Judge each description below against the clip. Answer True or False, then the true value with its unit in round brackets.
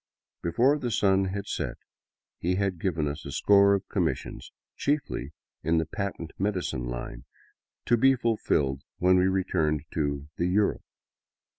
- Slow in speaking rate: False (150 wpm)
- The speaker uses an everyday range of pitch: True (4.6 semitones)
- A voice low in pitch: True (95 Hz)